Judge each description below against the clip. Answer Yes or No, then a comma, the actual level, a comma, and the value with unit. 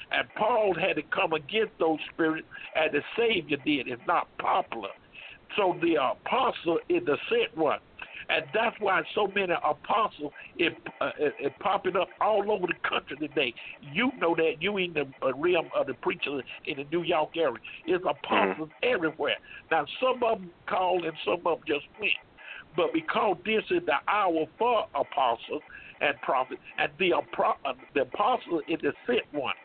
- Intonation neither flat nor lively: No, wide, 7.7 semitones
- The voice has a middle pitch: No, high, 195 Hz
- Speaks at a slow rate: No, average, 180 wpm